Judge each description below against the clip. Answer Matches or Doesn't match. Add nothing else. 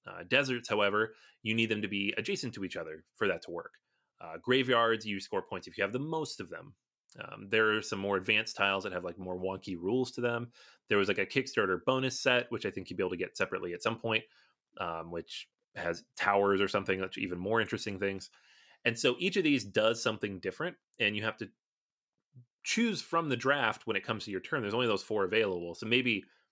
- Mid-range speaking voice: Doesn't match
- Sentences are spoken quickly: Matches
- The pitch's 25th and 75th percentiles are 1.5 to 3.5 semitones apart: Doesn't match